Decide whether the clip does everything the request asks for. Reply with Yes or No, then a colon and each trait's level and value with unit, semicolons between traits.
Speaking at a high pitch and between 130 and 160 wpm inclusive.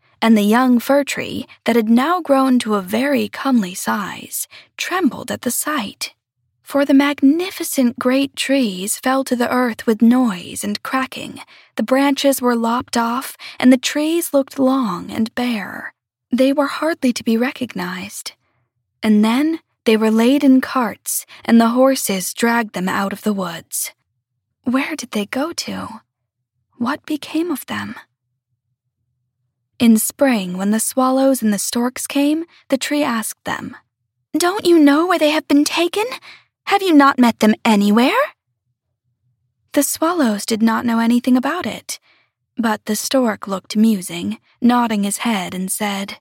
Yes: high, 240 Hz; average, 155 wpm